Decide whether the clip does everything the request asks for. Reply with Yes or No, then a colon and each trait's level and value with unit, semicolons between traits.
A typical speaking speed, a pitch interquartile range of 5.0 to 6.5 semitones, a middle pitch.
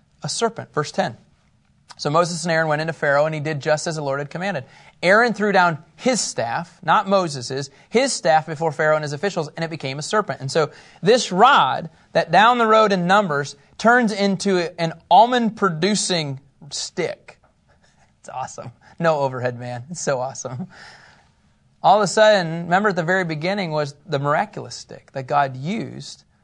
Yes: average, 180 wpm; wide, 5.4 semitones; medium, 165 Hz